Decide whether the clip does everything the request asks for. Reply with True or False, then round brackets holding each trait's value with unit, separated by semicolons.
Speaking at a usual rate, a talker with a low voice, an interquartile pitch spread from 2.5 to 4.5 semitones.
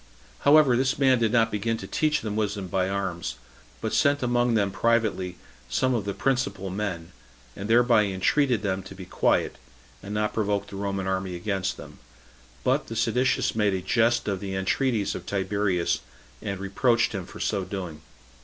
True (175 wpm; 105 Hz; 3.6 semitones)